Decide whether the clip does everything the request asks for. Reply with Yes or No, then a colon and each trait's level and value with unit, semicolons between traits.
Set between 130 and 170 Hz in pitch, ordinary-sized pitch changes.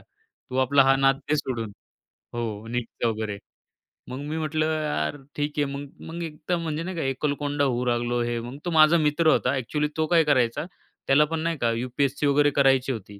Yes: medium, 140 Hz; average, 4.0 semitones